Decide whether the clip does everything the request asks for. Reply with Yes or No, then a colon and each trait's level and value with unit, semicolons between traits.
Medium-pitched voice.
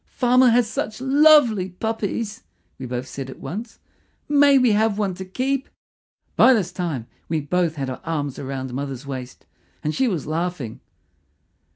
Yes: medium, 180 Hz